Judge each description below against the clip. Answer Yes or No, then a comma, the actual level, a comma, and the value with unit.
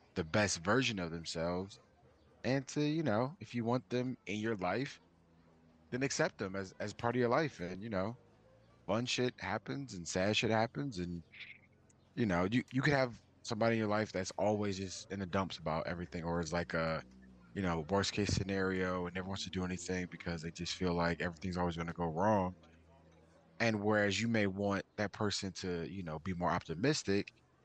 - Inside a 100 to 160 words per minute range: No, average, 200 wpm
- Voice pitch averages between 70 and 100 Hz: Yes, very low, 95 Hz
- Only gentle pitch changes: No, average, 4.4 semitones